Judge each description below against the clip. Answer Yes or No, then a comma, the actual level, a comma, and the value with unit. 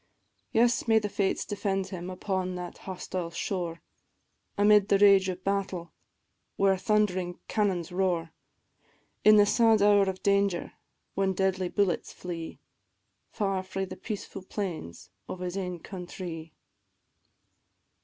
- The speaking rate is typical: No, slow, 125 wpm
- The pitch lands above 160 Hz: Yes, high, 190 Hz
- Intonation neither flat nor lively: No, narrow, 2.1 semitones